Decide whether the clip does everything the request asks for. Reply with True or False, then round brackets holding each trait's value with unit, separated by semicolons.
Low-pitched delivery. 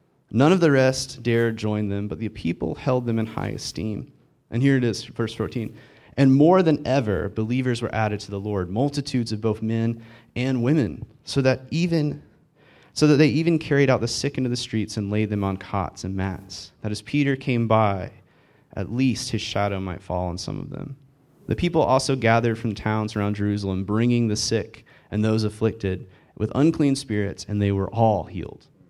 True (115 Hz)